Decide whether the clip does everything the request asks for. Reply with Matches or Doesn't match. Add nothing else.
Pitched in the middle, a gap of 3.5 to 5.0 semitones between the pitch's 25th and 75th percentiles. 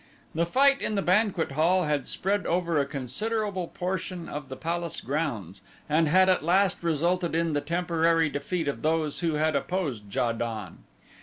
Matches